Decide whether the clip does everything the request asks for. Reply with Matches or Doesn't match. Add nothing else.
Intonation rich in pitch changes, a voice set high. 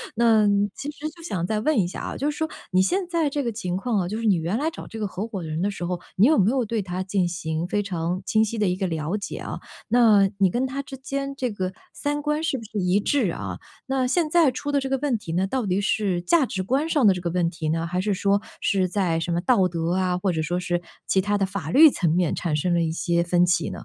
Matches